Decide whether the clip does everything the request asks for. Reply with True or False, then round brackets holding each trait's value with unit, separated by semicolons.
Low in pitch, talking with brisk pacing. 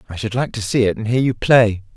True (110 Hz; 305 wpm)